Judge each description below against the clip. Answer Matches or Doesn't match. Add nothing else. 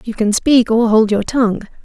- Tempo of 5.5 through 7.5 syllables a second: Doesn't match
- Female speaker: Matches